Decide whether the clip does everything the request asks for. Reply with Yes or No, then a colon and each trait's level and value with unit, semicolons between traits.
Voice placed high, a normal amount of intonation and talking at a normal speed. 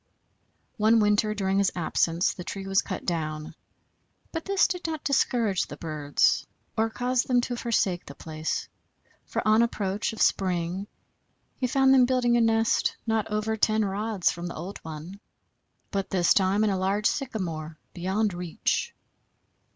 Yes: high, 205 Hz; average, 4.2 semitones; average, 160 wpm